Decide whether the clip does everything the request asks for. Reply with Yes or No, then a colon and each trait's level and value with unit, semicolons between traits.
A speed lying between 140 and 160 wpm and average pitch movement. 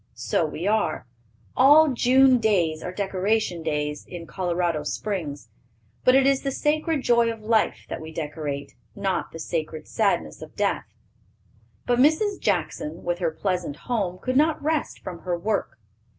No: average, 155 wpm; wide, 7.4 semitones